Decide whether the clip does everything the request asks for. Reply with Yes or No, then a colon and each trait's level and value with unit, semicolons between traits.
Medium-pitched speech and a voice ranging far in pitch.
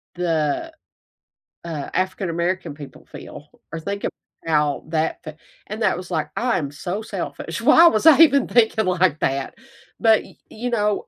Yes: medium, 180 Hz; wide, 5.8 semitones